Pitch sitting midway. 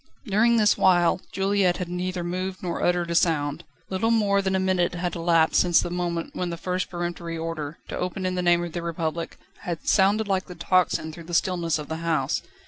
Yes: medium, 175 Hz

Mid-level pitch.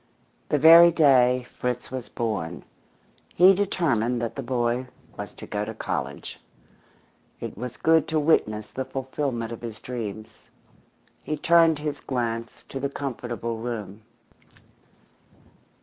No: low, 125 Hz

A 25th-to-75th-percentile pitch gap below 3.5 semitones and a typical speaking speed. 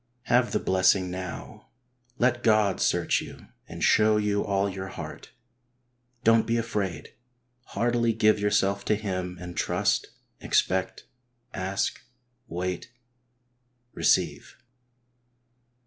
No: average, 3.1 semitones; slow, 105 wpm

